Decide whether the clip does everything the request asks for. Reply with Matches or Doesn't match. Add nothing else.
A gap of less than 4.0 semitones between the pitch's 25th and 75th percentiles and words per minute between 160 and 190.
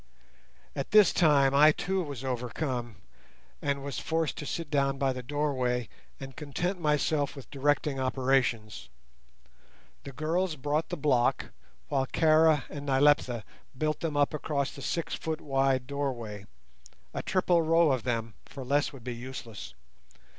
Doesn't match